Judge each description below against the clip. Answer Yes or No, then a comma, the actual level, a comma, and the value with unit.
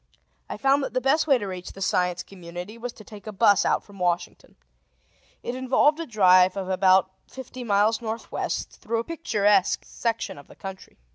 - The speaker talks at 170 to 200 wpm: Yes, average, 190 wpm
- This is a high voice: Yes, high, 210 Hz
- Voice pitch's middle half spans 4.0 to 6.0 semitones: Yes, average, 4.7 semitones